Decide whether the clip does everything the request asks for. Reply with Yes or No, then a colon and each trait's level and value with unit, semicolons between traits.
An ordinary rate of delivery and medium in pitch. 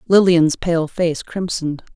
No: slow, 125 wpm; medium, 170 Hz